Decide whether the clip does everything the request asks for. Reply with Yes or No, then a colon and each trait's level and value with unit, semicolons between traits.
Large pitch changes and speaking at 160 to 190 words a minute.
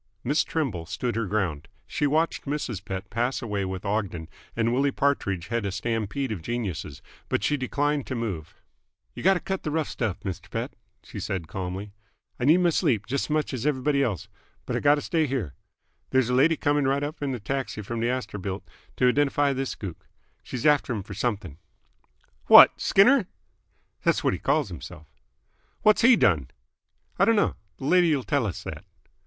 Yes: wide, 6.6 semitones; average, 180 wpm